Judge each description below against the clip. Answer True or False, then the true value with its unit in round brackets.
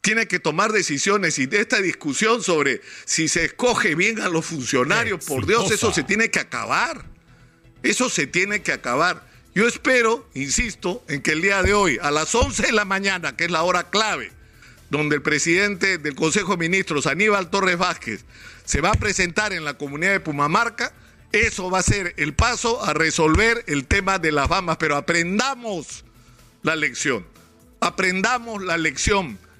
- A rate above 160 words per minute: True (175 wpm)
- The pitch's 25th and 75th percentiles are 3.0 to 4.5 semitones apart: False (4.9 semitones)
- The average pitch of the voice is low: False (185 Hz)